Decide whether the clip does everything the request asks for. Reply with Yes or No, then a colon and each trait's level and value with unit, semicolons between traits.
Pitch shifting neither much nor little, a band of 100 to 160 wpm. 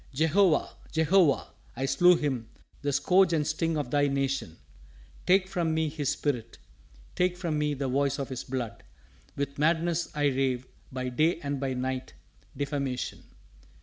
Yes: average, 3.4 semitones; average, 150 wpm